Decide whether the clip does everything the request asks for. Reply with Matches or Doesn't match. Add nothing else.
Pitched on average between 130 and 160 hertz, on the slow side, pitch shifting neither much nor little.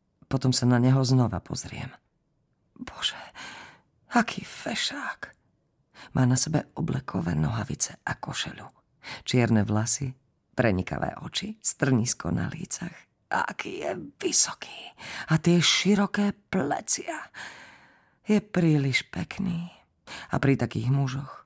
Doesn't match